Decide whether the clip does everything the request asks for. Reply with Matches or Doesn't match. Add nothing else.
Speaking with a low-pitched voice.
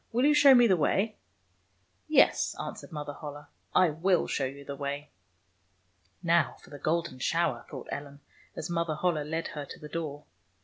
Doesn't match